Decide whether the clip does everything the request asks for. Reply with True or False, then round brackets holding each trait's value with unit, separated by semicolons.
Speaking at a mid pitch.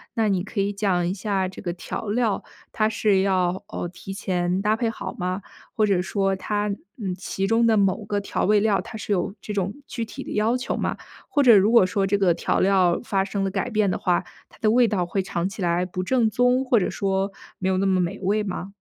False (195 Hz)